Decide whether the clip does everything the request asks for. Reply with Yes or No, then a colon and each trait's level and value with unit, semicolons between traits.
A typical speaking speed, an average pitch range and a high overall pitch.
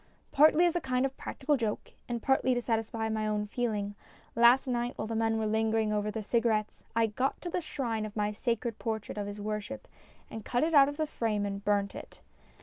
No: fast, 225 wpm; average, 3.2 semitones; high, 225 Hz